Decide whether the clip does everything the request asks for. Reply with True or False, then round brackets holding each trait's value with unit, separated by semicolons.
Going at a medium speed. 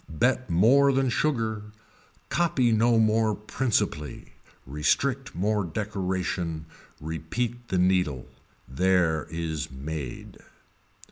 False (90 wpm)